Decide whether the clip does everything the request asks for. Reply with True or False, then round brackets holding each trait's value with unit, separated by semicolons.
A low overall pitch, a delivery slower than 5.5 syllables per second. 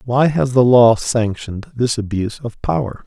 True (120 Hz; 4.8 syllables/s)